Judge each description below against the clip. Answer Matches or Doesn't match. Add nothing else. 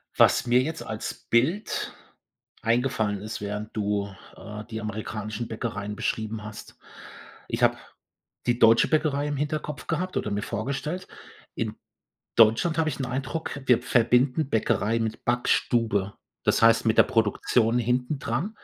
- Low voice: Matches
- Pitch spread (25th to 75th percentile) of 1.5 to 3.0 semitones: Doesn't match